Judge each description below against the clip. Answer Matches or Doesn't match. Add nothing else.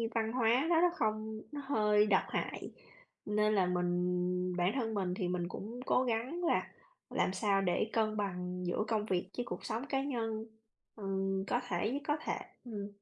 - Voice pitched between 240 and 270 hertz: Doesn't match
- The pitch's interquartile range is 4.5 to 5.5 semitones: Doesn't match